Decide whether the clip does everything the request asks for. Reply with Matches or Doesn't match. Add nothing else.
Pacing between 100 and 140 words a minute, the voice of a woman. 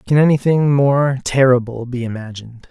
Doesn't match